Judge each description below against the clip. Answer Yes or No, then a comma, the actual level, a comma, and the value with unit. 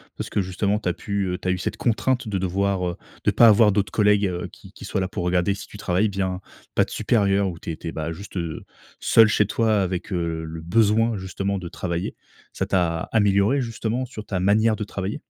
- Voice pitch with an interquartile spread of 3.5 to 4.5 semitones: No, average, 2.8 semitones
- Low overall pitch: Yes, low, 100 Hz